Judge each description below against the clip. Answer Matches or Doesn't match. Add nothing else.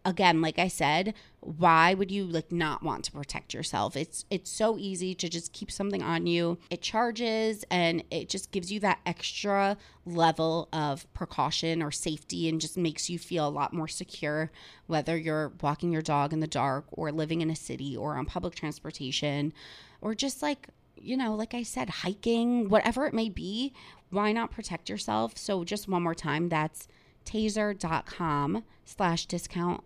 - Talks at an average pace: Matches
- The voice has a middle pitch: Matches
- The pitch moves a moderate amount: Matches